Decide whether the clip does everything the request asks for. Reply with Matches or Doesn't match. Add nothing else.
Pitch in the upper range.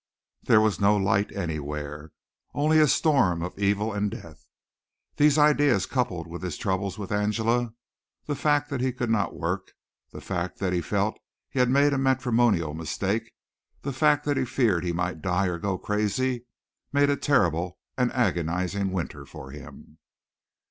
Doesn't match